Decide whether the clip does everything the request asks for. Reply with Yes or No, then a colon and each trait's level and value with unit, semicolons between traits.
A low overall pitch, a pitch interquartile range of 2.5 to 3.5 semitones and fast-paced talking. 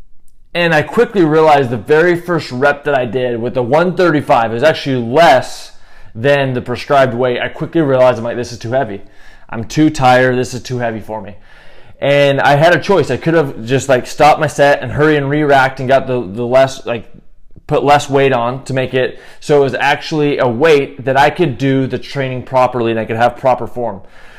Yes: low, 130 Hz; average, 3.1 semitones; fast, 215 wpm